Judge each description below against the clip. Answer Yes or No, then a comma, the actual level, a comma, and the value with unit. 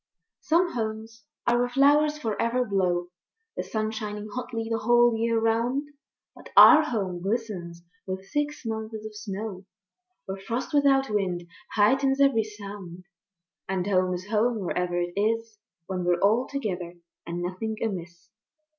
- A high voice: Yes, high, 220 Hz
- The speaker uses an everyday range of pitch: Yes, average, 4.2 semitones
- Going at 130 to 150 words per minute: Yes, average, 145 wpm